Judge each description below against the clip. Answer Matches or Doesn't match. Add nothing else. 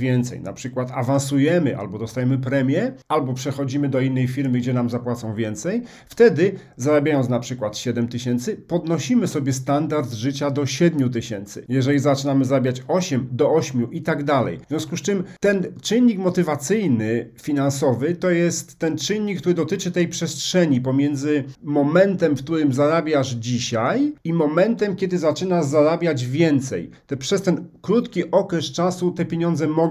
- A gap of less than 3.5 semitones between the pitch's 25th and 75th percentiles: Doesn't match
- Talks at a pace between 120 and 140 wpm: Doesn't match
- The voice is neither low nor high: Matches